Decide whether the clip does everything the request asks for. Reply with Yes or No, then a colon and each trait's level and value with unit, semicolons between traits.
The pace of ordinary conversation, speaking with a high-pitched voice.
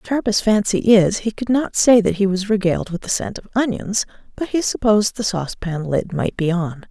No: fast, 225 wpm; high, 200 Hz